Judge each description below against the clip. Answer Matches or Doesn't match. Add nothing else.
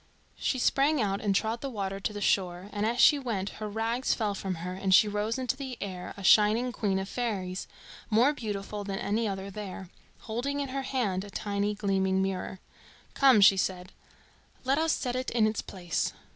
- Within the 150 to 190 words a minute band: Doesn't match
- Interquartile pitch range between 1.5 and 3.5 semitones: Doesn't match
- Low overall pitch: Doesn't match